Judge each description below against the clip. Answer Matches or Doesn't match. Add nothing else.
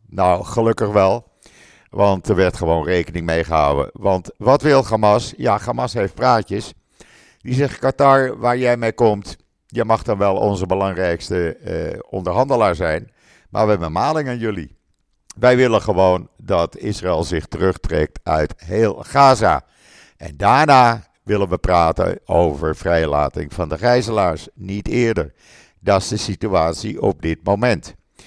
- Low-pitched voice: Matches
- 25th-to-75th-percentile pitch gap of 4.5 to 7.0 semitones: Matches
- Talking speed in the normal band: Matches